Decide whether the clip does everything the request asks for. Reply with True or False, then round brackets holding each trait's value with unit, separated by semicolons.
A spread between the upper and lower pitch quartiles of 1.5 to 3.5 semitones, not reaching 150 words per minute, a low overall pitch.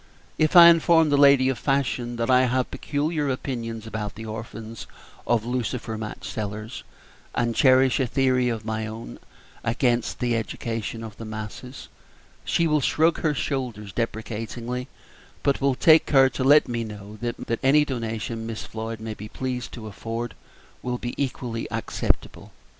False (3.0 semitones; 160 wpm; 120 Hz)